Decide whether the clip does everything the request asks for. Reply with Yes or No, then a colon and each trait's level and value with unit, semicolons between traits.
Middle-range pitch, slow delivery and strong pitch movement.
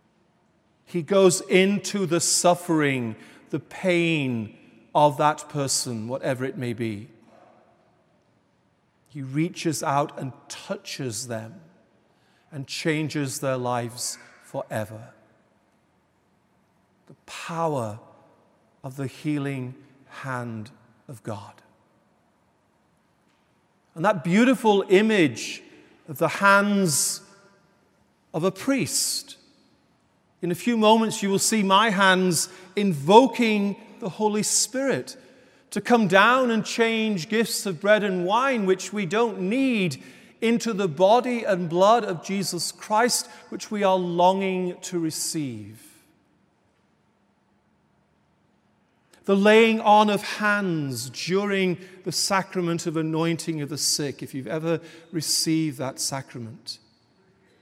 Yes: medium, 175 Hz; slow, 105 wpm; wide, 6.2 semitones